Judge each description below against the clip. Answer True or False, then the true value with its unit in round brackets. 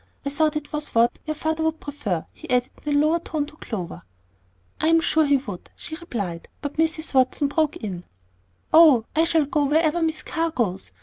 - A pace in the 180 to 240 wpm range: True (200 wpm)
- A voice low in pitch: False (295 Hz)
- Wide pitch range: False (4.2 semitones)